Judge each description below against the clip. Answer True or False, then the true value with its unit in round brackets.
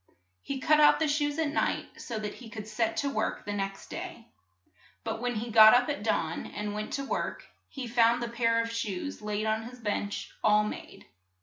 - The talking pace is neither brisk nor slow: False (210 wpm)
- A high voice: True (230 Hz)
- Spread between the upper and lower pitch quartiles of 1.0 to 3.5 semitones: True (2.9 semitones)